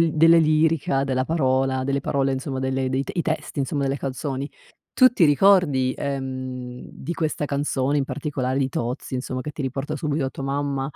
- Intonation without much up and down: Yes, narrow, 2.3 semitones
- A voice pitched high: No, low, 135 Hz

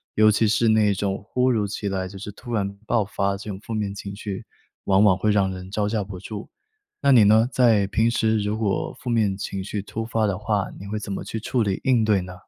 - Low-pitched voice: Yes, low, 105 Hz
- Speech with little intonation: Yes, narrow, 2.0 semitones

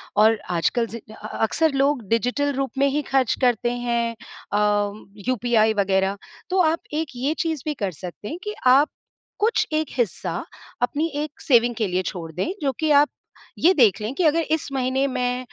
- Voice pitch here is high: Yes, very high, 250 Hz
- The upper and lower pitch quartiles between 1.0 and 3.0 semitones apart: No, average, 5.1 semitones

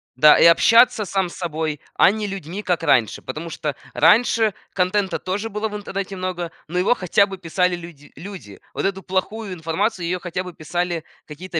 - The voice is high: No, medium, 180 Hz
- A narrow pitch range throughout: No, average, 3.1 semitones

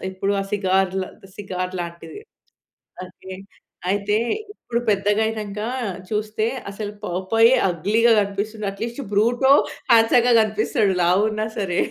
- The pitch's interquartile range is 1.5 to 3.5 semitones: Yes, narrow, 2.5 semitones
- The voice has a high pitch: Yes, high, 205 Hz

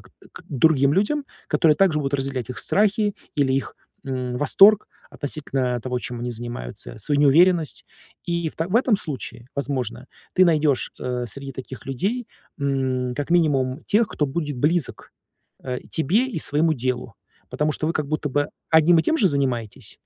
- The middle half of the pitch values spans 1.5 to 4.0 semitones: No, average, 4.6 semitones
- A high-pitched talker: No, medium, 145 Hz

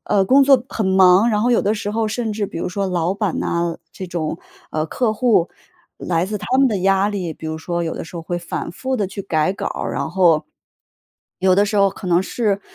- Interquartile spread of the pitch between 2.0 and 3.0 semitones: No, average, 3.6 semitones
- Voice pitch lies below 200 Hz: Yes, high, 190 Hz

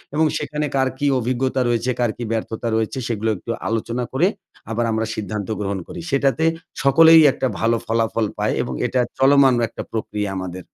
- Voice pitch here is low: Yes, low, 120 Hz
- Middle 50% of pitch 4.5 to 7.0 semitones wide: No, average, 3.3 semitones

